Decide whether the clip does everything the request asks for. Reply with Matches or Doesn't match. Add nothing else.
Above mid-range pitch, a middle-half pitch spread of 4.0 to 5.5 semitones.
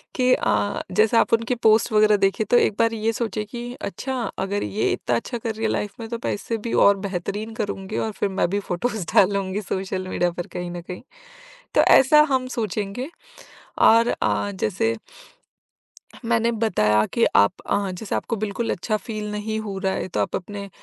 Doesn't match